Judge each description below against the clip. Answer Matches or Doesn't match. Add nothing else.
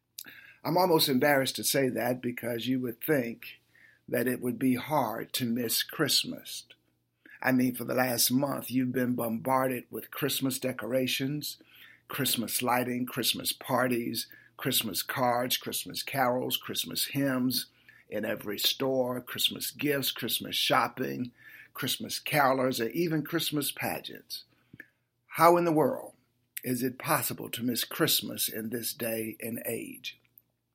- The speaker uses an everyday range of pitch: Doesn't match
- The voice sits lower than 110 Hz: Doesn't match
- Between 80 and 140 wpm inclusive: Matches